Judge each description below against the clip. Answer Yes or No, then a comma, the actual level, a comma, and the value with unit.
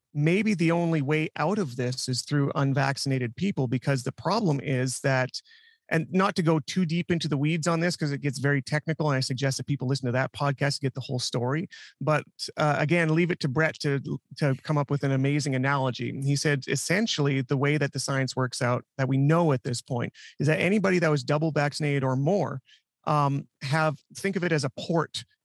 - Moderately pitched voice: Yes, medium, 145 Hz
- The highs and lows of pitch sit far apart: No, average, 3.1 semitones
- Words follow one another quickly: Yes, fast, 220 wpm